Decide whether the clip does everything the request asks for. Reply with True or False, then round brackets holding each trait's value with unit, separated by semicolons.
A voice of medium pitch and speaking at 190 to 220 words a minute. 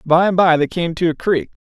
False (170 Hz; 285 wpm)